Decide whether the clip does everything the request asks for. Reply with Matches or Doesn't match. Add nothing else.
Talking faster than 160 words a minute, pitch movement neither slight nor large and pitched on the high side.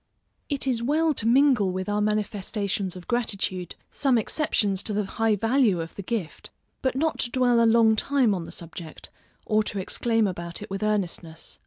Matches